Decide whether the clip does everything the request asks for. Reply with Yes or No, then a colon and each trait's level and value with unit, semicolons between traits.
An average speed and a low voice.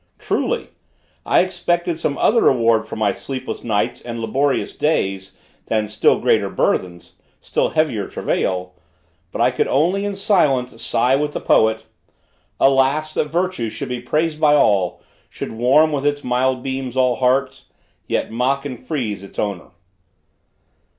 Yes: average, 150 wpm; low, 130 Hz